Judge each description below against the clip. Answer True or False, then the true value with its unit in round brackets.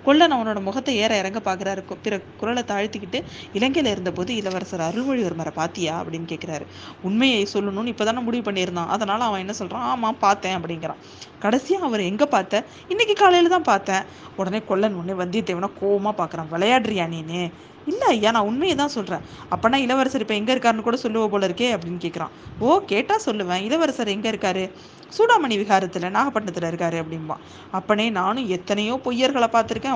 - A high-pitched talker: True (205 Hz)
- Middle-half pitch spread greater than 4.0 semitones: True (4.7 semitones)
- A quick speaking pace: True (160 wpm)